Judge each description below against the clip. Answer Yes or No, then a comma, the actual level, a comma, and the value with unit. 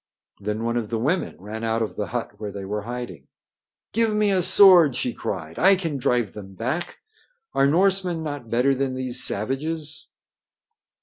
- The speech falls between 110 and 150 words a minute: No, average, 175 wpm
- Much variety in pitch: Yes, wide, 6.7 semitones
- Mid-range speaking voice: No, low, 125 Hz